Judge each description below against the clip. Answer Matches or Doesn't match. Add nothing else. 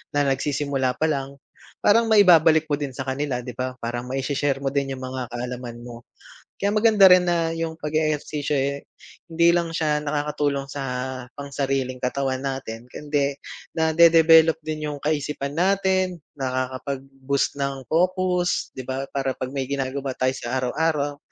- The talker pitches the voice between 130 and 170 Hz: Matches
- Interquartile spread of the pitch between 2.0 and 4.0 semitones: Matches